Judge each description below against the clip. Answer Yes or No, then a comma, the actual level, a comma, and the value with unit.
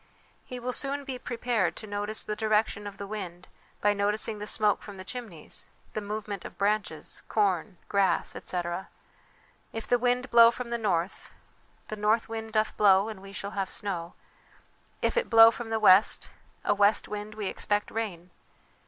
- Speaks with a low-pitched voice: No, high, 210 Hz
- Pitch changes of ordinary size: No, narrow, 2.3 semitones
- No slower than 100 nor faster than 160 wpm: No, average, 175 wpm